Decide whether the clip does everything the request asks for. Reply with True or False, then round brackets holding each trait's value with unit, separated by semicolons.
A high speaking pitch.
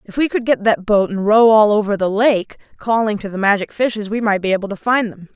True (210 Hz)